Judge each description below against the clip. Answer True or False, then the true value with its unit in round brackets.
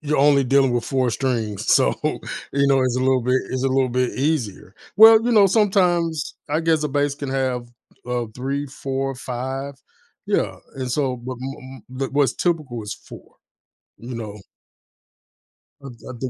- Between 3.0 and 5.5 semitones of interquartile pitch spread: False (2.5 semitones)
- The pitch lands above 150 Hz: False (135 Hz)